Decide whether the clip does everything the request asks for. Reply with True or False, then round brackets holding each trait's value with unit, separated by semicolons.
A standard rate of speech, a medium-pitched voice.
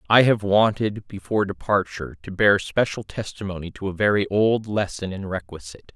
False (160 wpm; 100 Hz)